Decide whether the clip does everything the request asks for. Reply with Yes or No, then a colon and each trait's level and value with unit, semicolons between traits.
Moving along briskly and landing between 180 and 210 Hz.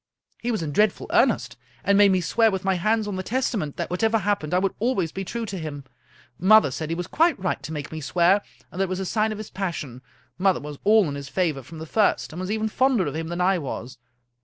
Yes: fast, 260 wpm; medium, 185 Hz